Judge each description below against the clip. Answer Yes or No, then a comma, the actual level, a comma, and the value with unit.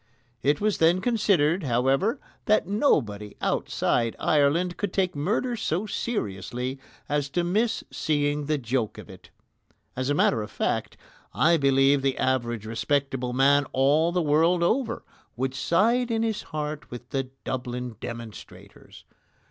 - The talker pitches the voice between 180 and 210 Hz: No, medium, 145 Hz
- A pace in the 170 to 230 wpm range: No, average, 140 wpm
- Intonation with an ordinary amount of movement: No, wide, 5.8 semitones